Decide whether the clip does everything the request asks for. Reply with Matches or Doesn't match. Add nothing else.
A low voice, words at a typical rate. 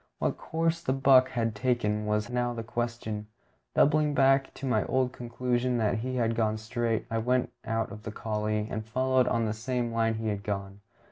Matches